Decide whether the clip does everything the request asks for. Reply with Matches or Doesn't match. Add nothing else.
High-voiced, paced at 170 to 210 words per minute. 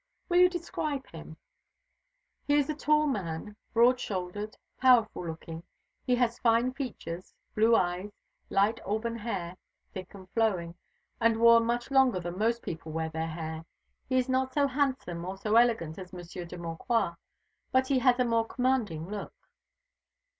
Doesn't match